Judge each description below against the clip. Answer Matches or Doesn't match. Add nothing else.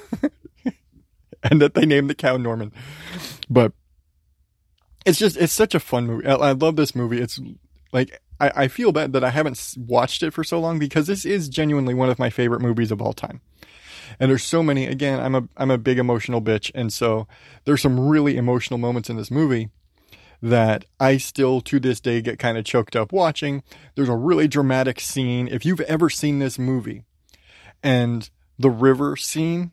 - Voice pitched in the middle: Doesn't match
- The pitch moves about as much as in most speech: Matches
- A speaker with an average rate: Matches